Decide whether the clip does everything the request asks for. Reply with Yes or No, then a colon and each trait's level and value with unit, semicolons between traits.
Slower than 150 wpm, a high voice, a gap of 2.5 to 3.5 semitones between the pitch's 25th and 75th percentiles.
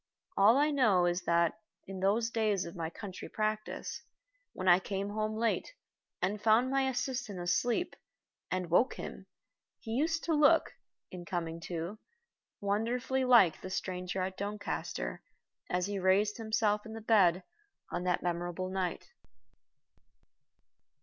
No: average, 140 wpm; high, 200 Hz; average, 4.0 semitones